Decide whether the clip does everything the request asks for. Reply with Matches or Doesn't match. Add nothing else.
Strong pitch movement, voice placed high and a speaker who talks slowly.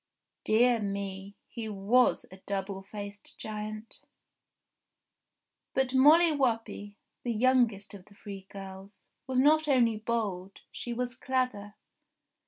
Doesn't match